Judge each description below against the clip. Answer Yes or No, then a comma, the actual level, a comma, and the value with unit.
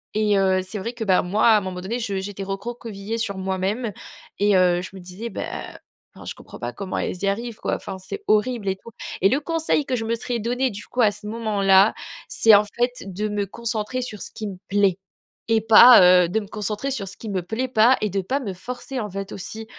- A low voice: No, high, 210 Hz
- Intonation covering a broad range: No, average, 3.1 semitones